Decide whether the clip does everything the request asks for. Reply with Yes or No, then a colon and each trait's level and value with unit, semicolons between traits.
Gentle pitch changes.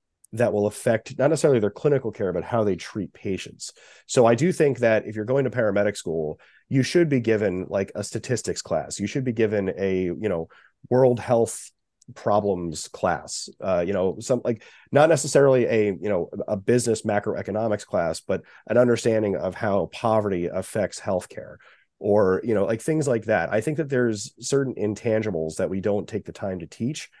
No: average, 3.3 semitones